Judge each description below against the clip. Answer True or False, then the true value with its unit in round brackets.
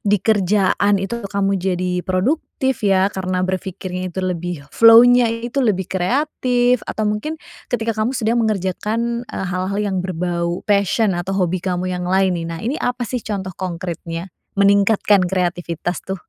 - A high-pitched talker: True (195 Hz)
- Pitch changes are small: False (3.6 semitones)